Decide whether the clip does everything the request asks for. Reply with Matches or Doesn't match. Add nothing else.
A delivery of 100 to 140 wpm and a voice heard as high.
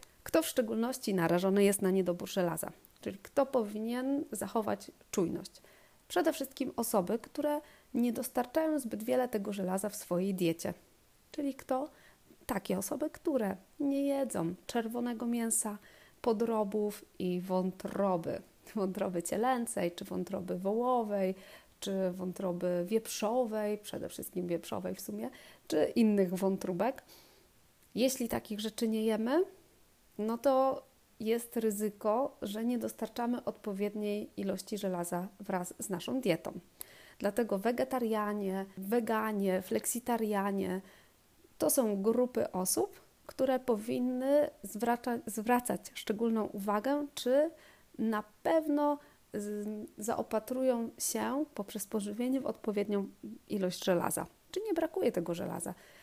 Matches